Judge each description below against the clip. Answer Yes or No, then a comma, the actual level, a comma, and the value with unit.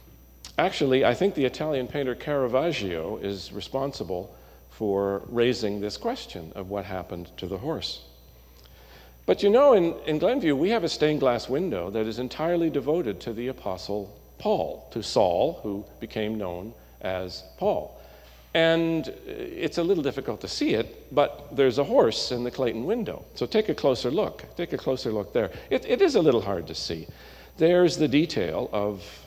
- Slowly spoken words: No, average, 170 wpm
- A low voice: Yes, low, 120 Hz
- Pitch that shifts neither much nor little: No, wide, 7.7 semitones